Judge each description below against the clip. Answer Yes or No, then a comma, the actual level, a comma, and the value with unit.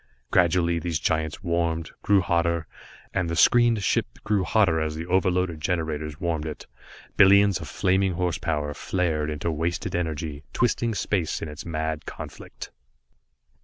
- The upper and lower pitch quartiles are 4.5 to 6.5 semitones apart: No, average, 2.8 semitones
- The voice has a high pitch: No, very low, 85 Hz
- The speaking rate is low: No, average, 145 wpm